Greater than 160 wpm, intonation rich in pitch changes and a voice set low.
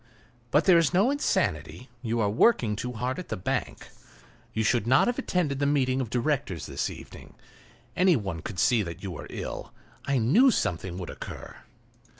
Yes: average, 180 wpm; wide, 7.6 semitones; low, 125 Hz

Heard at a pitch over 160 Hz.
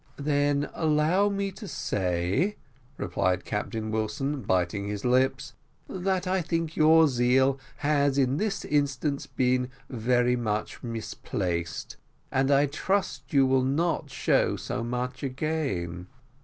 No: low, 135 Hz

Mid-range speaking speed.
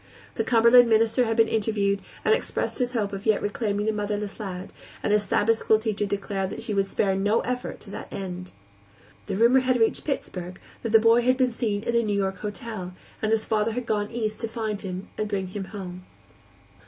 No: fast, 215 wpm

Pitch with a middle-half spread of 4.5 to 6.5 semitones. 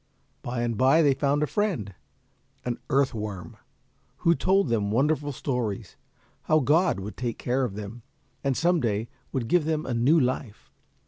Yes: average, 4.8 semitones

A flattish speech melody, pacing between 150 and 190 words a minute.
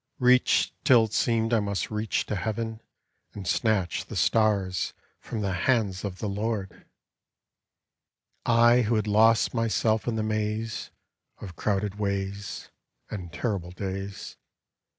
No: narrow, 2.3 semitones; slow, 135 wpm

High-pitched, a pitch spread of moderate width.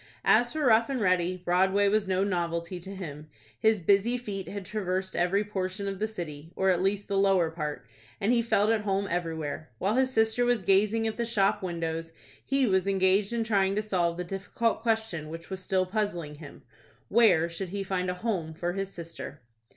Yes: high, 195 Hz; average, 3.5 semitones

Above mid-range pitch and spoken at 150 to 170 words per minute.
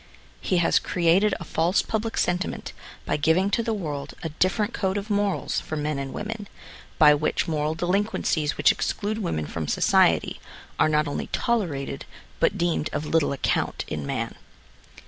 No: medium, 170 Hz; average, 165 wpm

